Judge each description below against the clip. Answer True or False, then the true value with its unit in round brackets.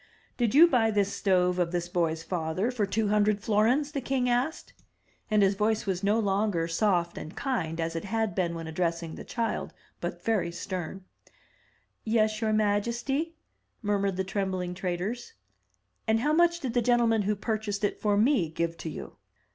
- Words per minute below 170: False (175 wpm)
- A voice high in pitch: True (205 Hz)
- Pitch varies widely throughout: False (4.2 semitones)